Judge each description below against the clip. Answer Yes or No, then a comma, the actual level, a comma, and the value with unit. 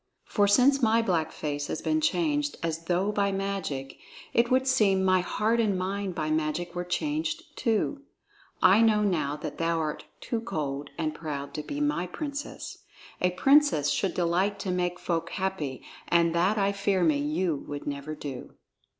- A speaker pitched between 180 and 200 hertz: Yes, medium, 185 Hz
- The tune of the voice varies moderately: No, wide, 5.9 semitones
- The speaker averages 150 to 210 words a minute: Yes, average, 175 wpm